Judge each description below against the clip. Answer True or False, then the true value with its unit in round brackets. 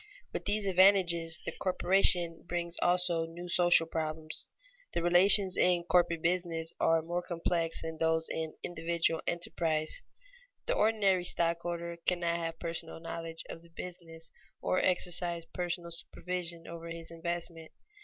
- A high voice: False (170 Hz)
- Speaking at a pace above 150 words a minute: False (135 wpm)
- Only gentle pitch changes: True (1.4 semitones)